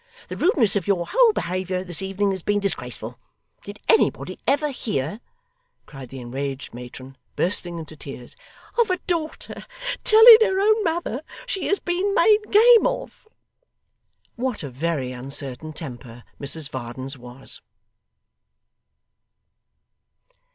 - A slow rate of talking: Yes, slow, 125 wpm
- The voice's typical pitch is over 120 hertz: Yes, medium, 185 Hz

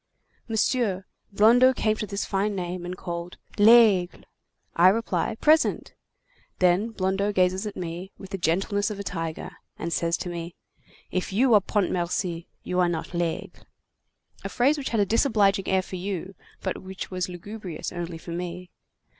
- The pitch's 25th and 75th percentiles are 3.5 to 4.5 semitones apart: No, average, 3.1 semitones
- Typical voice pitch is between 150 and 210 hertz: Yes, high, 190 Hz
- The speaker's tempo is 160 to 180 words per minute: Yes, average, 165 wpm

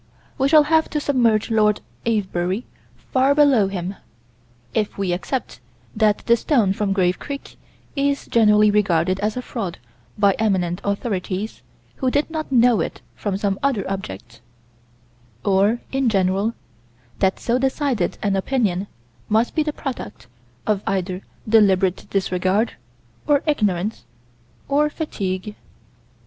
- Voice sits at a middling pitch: No, high, 210 Hz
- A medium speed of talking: No, slow, 130 wpm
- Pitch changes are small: No, average, 5.1 semitones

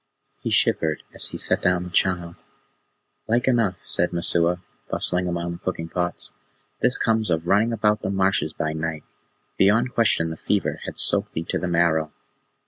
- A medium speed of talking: Yes, average, 170 wpm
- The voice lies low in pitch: Yes, very low, 90 Hz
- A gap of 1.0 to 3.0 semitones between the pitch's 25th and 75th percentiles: No, average, 3.6 semitones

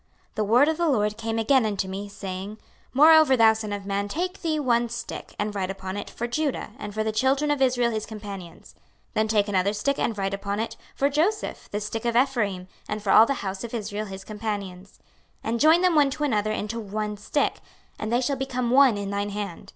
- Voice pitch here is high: Yes, high, 220 Hz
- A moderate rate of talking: No, fast, 230 wpm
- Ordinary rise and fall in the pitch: Yes, average, 4.4 semitones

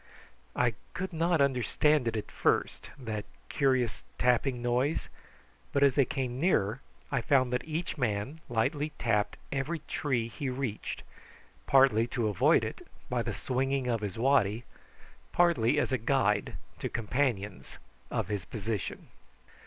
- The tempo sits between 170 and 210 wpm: No, average, 140 wpm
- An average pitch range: Yes, average, 3.7 semitones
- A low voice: Yes, low, 125 Hz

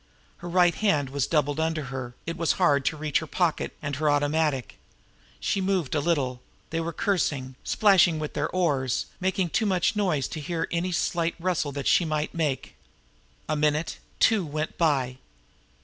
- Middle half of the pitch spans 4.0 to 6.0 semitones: No, average, 3.4 semitones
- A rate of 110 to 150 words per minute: No, average, 175 wpm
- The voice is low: No, medium, 155 Hz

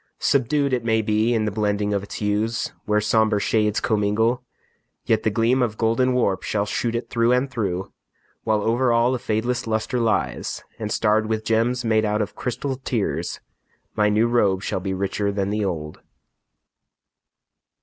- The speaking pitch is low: Yes, low, 110 Hz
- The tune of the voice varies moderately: No, narrow, 2.2 semitones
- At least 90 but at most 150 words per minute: No, average, 170 wpm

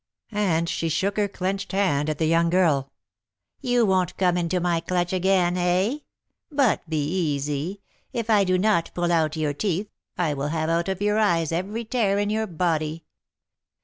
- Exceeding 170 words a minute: Yes, average, 180 wpm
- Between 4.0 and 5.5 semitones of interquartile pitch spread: No, average, 3.6 semitones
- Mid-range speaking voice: Yes, medium, 180 Hz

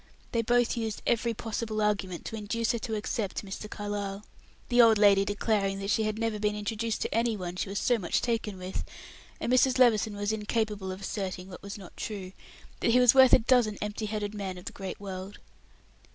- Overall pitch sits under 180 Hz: No, high, 210 Hz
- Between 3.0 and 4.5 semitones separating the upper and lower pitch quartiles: No, narrow, 2.5 semitones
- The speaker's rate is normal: No, fast, 210 wpm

